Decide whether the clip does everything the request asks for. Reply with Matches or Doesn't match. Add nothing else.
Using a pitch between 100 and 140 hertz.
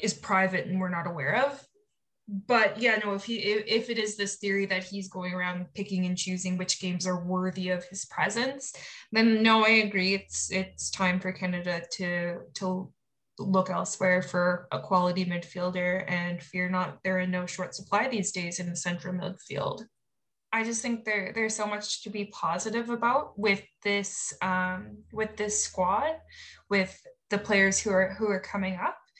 Doesn't match